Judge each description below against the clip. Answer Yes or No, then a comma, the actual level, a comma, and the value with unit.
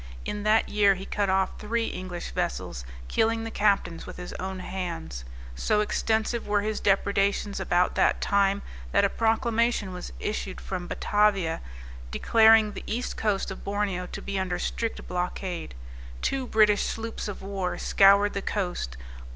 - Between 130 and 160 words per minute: Yes, average, 155 wpm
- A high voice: Yes, high, 200 Hz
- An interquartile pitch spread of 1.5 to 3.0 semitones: Yes, narrow, 2.6 semitones